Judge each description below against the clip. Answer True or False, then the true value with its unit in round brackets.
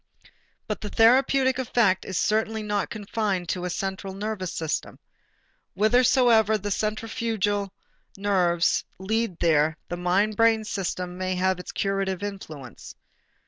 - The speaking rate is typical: False (125 wpm)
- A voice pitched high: True (200 Hz)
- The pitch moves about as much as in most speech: True (3.0 semitones)